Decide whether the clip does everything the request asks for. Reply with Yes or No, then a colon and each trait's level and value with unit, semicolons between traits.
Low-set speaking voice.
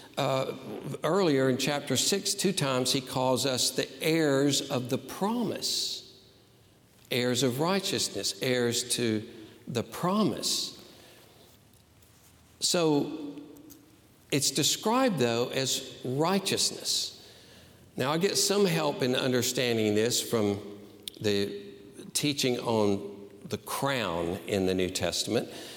Yes: low, 125 Hz